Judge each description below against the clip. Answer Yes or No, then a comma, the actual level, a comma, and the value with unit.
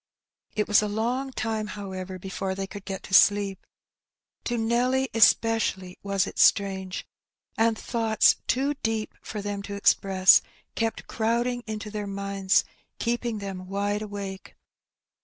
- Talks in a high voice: Yes, high, 205 Hz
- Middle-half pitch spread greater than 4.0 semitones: No, narrow, 2.5 semitones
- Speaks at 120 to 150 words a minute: Yes, average, 140 wpm